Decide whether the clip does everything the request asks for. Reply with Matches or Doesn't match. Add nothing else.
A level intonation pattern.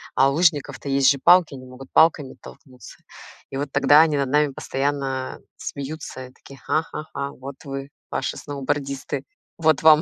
Matches